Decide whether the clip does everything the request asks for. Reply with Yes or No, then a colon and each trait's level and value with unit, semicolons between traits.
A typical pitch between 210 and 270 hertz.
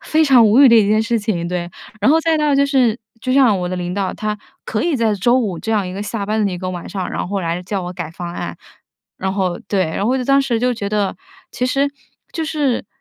Yes: high, 215 Hz